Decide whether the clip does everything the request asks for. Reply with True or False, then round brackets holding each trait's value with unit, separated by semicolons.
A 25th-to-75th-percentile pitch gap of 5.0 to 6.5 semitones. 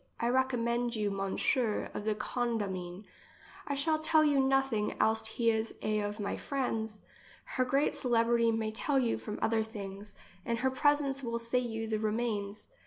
False (3.2 semitones)